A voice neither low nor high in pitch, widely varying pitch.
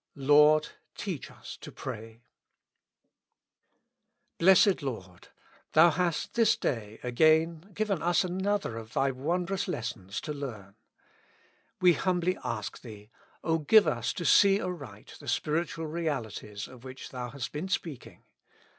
Yes: medium, 150 Hz; wide, 6.7 semitones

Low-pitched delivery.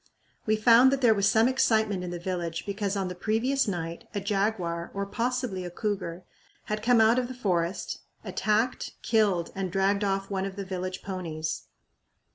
No: high, 200 Hz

